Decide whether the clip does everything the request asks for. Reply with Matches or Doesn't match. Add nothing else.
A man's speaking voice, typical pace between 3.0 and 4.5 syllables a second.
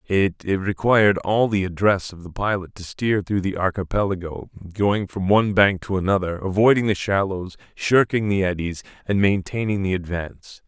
Doesn't match